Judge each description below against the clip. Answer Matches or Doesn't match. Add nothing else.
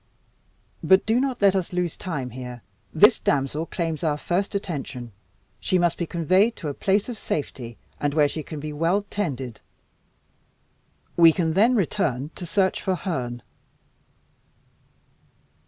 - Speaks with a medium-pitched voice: Matches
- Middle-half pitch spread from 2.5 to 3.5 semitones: Doesn't match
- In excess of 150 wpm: Doesn't match